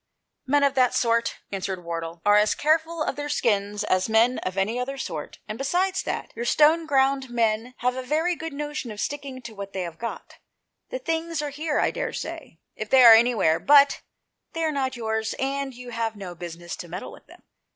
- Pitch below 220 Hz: No, very high, 250 Hz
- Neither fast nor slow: No, fast, 210 wpm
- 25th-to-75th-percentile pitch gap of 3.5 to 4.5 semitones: No, wide, 5.6 semitones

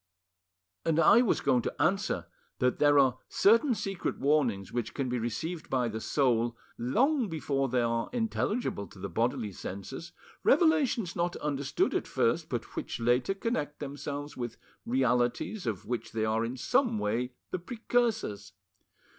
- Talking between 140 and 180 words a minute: Yes, average, 155 wpm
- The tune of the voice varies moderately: No, wide, 7.7 semitones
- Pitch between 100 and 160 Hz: Yes, low, 135 Hz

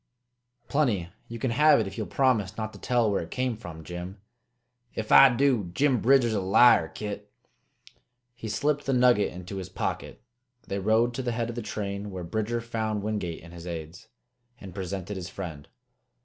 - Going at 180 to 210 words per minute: Yes, average, 185 wpm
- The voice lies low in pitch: Yes, low, 105 Hz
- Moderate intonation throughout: Yes, average, 4.3 semitones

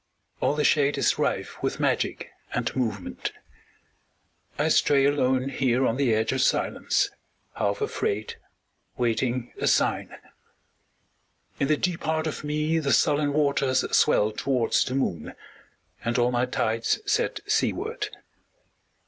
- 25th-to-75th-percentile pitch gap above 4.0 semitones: No, average, 3.7 semitones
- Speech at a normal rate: No, slow, 130 wpm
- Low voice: Yes, low, 130 Hz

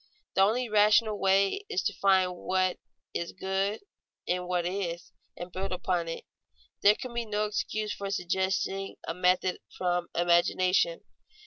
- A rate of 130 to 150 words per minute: Yes, average, 145 wpm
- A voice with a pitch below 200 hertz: Yes, high, 190 Hz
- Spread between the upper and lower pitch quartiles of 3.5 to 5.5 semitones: No, narrow, 2.4 semitones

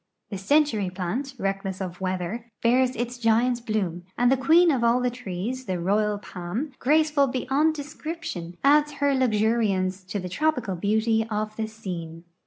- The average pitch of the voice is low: No, high, 225 Hz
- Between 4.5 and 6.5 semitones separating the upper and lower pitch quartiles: Yes, wide, 5.4 semitones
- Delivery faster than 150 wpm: Yes, average, 160 wpm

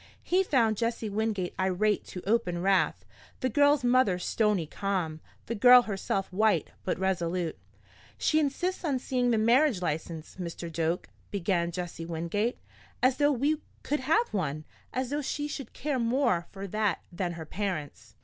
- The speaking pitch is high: Yes, high, 210 Hz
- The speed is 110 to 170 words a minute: Yes, average, 160 wpm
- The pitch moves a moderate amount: No, wide, 6.4 semitones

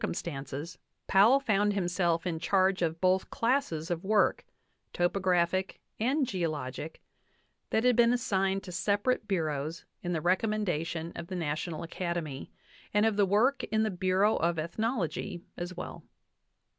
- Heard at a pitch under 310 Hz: Yes, medium, 185 Hz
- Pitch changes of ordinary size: Yes, average, 3.7 semitones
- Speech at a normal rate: Yes, average, 145 wpm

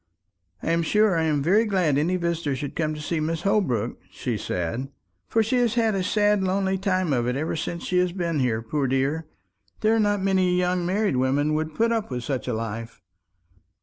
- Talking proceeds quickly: Yes, fast, 210 wpm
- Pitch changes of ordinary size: No, wide, 6.1 semitones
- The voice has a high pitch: No, medium, 165 Hz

